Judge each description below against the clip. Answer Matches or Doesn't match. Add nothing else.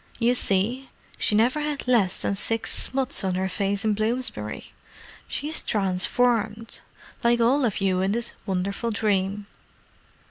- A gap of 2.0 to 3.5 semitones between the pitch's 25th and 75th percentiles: Doesn't match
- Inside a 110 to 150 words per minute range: Matches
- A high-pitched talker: Matches